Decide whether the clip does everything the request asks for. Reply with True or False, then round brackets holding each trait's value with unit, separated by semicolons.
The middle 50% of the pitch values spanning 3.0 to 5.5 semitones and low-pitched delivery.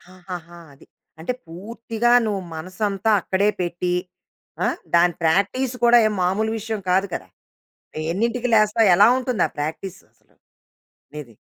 False (4.1 semitones; 195 Hz)